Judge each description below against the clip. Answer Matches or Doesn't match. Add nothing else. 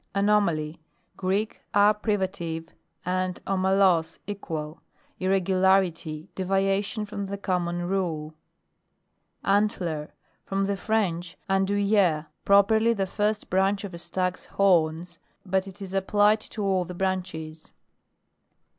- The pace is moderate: Doesn't match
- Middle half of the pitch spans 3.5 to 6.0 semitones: Doesn't match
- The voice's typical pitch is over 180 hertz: Matches